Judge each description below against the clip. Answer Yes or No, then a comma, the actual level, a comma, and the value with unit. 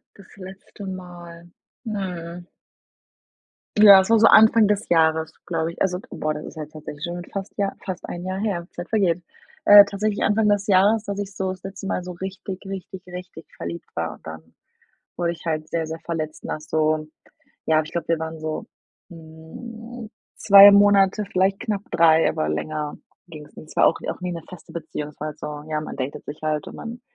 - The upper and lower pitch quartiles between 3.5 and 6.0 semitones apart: Yes, average, 3.9 semitones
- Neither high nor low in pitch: Yes, medium, 175 Hz